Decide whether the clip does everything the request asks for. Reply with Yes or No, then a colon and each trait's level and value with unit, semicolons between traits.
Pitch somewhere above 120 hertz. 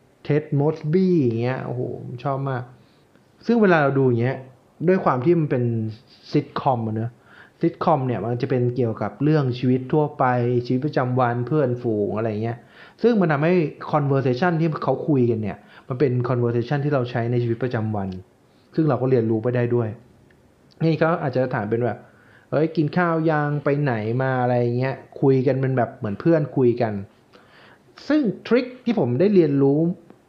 Yes: low, 130 Hz